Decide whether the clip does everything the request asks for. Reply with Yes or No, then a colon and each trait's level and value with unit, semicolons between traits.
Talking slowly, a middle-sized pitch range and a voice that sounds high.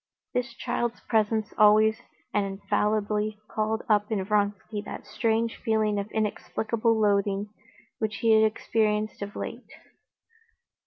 No: slow, 120 wpm; narrow, 1.1 semitones; high, 215 Hz